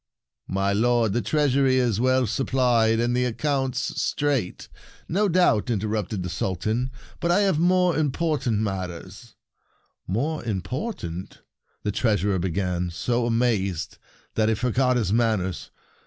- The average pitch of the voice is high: No, low, 115 Hz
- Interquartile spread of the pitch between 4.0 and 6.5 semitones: Yes, average, 4.8 semitones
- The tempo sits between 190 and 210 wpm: No, average, 155 wpm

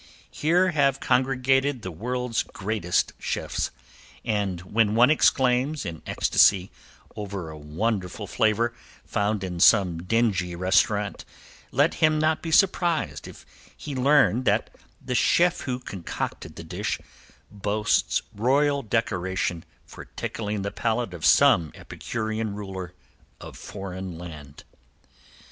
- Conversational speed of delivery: No, slow, 120 wpm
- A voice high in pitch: No, low, 110 Hz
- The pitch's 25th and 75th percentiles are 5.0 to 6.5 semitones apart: Yes, wide, 5.5 semitones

